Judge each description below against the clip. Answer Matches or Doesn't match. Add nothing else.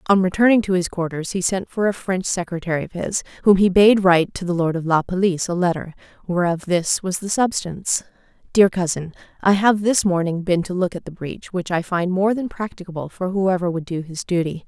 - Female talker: Matches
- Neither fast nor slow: Doesn't match